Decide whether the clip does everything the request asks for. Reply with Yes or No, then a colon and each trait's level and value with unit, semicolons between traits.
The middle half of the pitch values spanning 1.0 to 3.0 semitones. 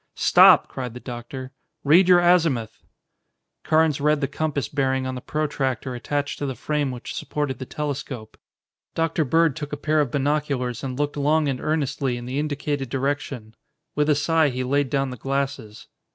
Yes: narrow, 2.5 semitones